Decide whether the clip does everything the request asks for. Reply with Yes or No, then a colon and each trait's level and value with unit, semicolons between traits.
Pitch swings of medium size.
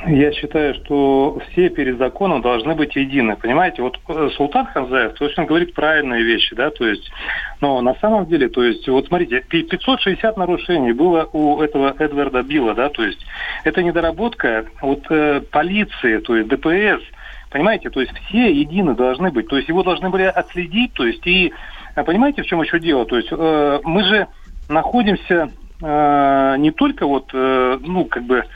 Yes: average, 4.8 semitones